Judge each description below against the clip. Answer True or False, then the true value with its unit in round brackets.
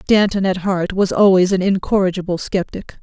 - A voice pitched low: False (190 Hz)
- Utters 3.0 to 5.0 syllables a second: False (5.2 syllables/s)